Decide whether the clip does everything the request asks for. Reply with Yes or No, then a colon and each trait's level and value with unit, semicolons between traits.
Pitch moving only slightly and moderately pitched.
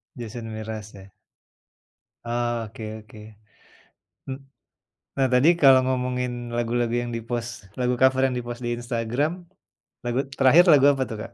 No: narrow, 2.1 semitones; low, 120 Hz